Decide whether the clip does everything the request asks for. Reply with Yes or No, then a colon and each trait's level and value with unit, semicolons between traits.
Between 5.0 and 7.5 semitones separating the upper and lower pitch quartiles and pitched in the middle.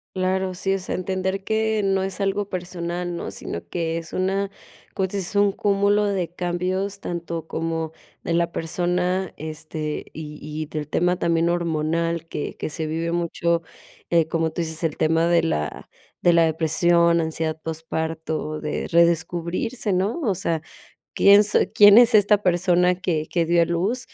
No: average, 2.7 semitones; medium, 170 Hz